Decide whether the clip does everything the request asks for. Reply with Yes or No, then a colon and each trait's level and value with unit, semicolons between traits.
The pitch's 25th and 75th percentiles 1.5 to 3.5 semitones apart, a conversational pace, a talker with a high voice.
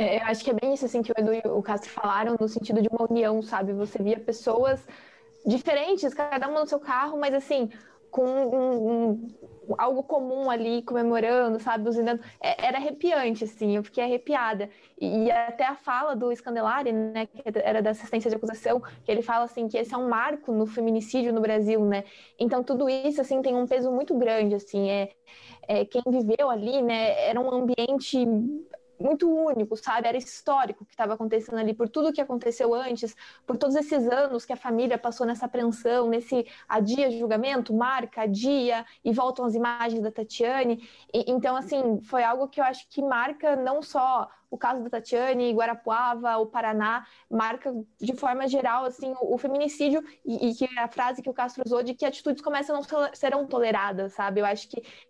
Yes: average, 2.9 semitones; average, 195 wpm; high, 245 Hz